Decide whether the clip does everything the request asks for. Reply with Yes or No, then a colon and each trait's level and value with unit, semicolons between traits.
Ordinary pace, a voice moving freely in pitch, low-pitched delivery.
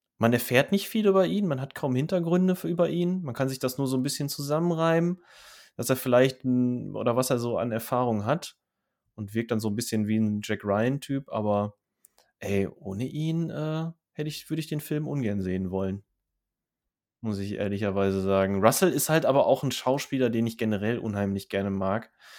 No: fast, 200 wpm; wide, 6.3 semitones; low, 125 Hz